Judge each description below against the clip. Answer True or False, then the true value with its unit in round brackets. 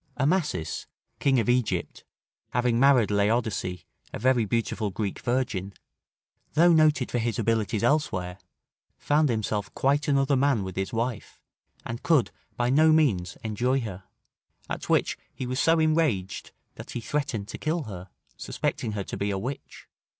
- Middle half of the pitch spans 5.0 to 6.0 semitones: True (5.4 semitones)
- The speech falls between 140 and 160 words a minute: True (150 wpm)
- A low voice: True (120 Hz)